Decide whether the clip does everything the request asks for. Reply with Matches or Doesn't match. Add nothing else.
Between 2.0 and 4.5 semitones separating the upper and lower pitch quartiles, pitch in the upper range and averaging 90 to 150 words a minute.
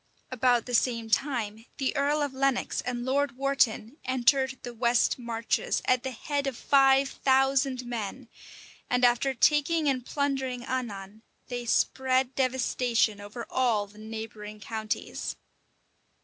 Matches